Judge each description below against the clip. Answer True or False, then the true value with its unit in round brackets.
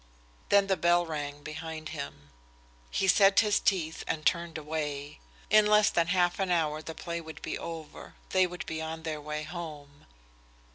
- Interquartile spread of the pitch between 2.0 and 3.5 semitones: True (2.7 semitones)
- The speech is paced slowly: False (175 wpm)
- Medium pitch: True (160 Hz)